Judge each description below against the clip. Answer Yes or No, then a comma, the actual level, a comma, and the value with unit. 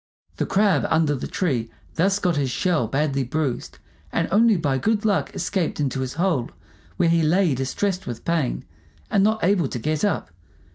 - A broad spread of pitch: Yes, wide, 6.2 semitones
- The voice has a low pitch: No, medium, 165 Hz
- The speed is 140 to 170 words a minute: No, average, 180 wpm